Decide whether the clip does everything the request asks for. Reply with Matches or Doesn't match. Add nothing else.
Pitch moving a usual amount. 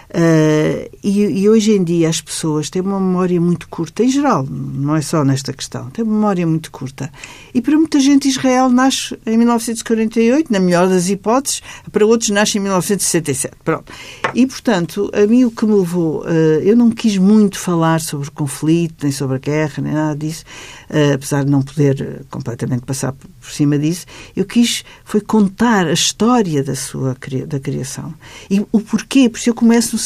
Doesn't match